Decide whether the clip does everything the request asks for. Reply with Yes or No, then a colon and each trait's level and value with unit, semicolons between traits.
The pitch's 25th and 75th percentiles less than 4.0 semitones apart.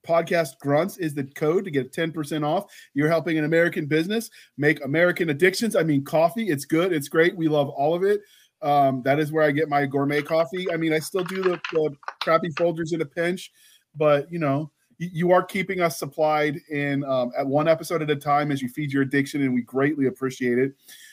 Yes: average, 3.1 semitones